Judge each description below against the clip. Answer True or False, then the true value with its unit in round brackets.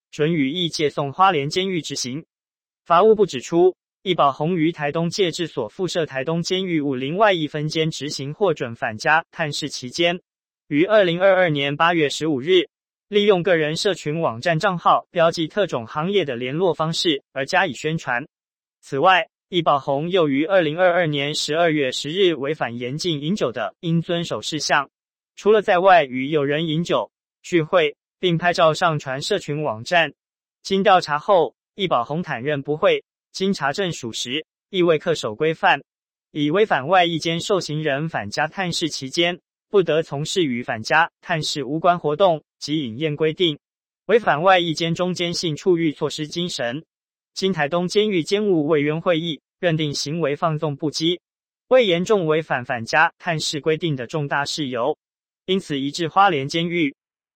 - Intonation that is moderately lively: True (3.5 semitones)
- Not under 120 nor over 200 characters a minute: False (255 characters per minute)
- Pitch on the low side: False (165 Hz)